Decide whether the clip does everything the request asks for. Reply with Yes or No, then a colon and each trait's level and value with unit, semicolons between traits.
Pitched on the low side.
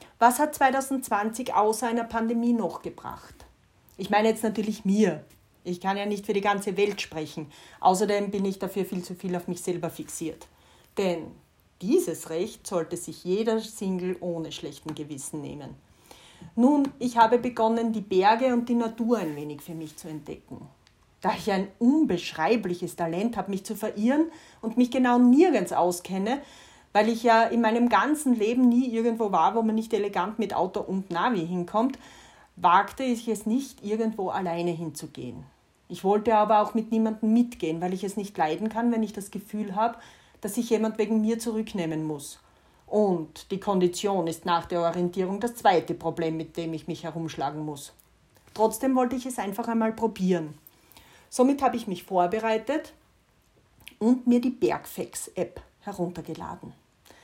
No: high, 205 Hz